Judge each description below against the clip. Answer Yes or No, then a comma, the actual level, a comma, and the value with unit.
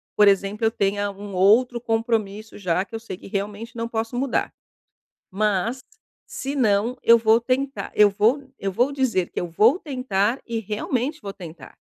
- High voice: Yes, high, 220 Hz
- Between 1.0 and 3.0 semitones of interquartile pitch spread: No, average, 3.4 semitones